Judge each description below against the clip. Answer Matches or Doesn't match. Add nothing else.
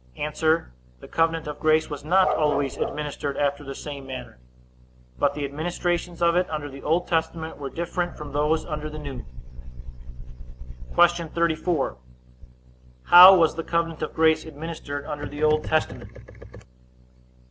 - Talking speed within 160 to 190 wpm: Doesn't match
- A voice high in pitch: Doesn't match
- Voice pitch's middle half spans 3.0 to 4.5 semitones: Doesn't match